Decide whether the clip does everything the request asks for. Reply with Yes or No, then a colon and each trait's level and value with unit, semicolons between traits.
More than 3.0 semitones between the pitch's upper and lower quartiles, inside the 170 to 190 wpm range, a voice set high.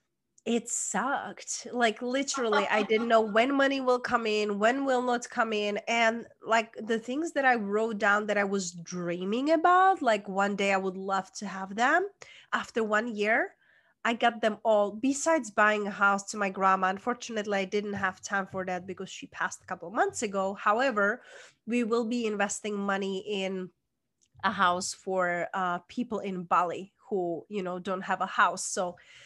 Yes: average, 3.6 semitones; average, 185 wpm; high, 210 Hz